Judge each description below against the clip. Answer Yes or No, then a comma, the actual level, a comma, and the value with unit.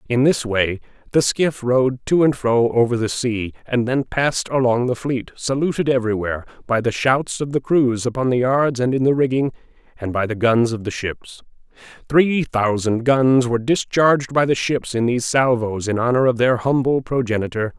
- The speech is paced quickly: No, average, 195 wpm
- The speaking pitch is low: Yes, low, 125 Hz